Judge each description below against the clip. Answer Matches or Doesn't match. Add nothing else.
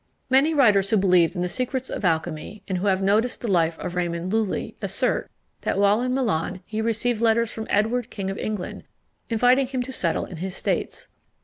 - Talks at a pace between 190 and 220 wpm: Matches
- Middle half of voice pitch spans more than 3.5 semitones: Matches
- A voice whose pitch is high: Matches